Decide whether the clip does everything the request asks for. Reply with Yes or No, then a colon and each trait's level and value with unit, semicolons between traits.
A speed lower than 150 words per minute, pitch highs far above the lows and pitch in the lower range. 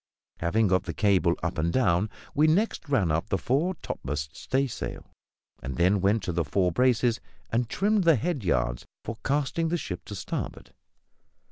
No: average, 170 wpm; wide, 8.0 semitones; low, 110 Hz